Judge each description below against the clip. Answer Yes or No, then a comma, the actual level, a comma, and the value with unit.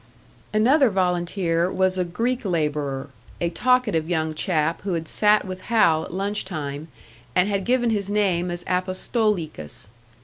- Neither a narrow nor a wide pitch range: Yes, average, 4.1 semitones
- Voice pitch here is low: No, medium, 185 Hz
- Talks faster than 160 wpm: No, average, 145 wpm